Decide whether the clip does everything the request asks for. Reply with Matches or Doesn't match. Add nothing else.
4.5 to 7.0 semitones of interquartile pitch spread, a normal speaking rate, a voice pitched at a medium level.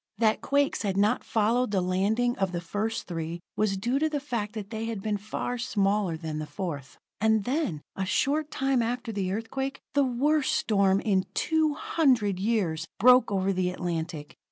Doesn't match